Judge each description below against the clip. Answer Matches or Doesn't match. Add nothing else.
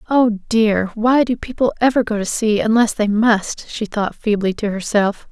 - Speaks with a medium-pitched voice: Doesn't match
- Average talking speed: Matches